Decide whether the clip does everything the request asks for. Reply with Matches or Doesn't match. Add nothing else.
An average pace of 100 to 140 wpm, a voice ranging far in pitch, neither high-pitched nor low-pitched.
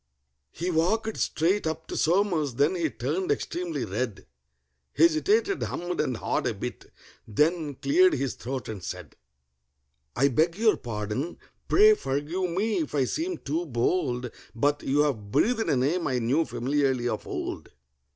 Doesn't match